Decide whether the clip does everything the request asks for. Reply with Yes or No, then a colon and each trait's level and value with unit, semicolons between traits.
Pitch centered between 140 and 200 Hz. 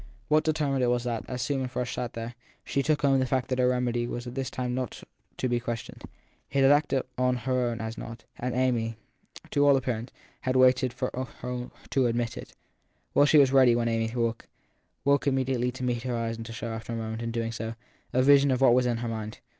No: low, 125 Hz